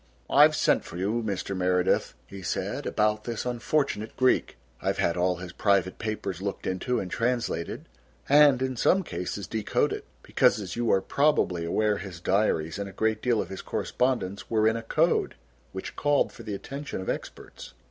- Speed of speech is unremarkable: Yes, average, 180 wpm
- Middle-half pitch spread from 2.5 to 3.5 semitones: No, average, 4.3 semitones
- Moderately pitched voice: No, low, 105 Hz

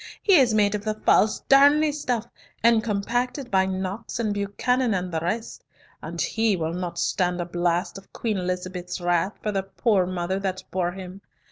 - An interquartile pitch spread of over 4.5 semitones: No, average, 4.0 semitones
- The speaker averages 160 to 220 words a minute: Yes, average, 180 wpm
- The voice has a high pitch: Yes, high, 195 Hz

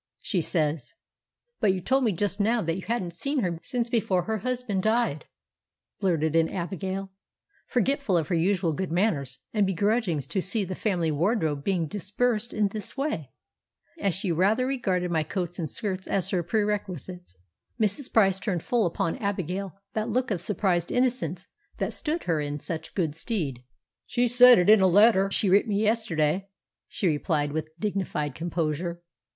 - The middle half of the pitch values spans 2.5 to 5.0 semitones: Yes, average, 4.5 semitones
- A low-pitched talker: No, high, 190 Hz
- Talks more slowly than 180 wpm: Yes, average, 170 wpm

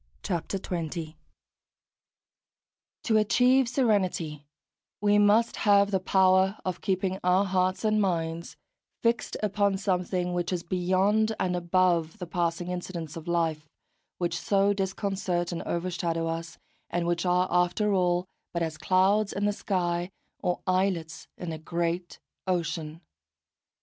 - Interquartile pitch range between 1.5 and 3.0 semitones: Yes, narrow, 2.5 semitones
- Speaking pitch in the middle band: Yes, medium, 180 Hz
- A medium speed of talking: No, slow, 130 wpm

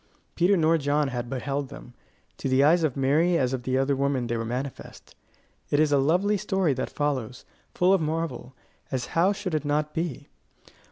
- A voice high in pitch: No, medium, 145 Hz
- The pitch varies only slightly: No, average, 4.0 semitones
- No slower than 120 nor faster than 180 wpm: No, average, 190 wpm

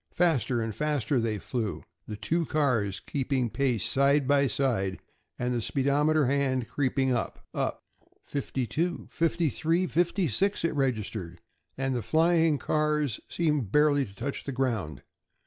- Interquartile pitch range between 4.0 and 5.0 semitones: Yes, average, 4.6 semitones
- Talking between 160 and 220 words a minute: No, average, 145 wpm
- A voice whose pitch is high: No, low, 135 Hz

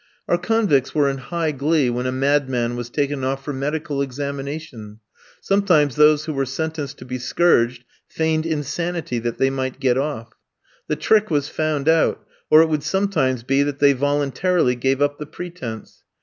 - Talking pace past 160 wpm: Yes, average, 175 wpm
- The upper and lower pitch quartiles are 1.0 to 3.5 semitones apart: Yes, average, 3.2 semitones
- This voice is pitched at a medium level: Yes, medium, 145 Hz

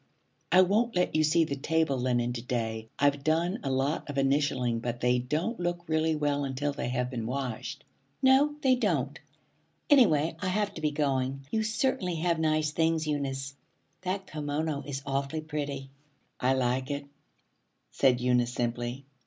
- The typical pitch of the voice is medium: Yes, medium, 145 Hz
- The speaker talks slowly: No, average, 165 wpm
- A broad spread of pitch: No, average, 3.8 semitones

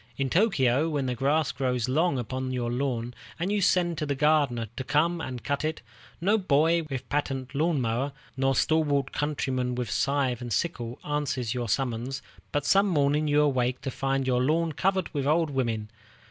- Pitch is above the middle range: No, medium, 140 Hz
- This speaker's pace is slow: No, average, 185 wpm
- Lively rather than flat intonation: No, average, 3.6 semitones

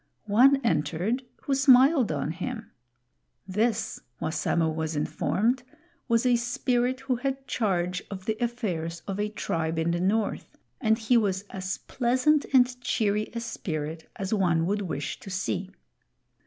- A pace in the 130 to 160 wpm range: Yes, average, 145 wpm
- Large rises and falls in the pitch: Yes, wide, 6.0 semitones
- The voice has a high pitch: Yes, high, 210 Hz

